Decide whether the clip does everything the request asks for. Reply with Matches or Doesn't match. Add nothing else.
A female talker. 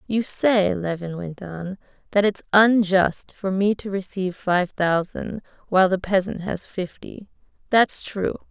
Matches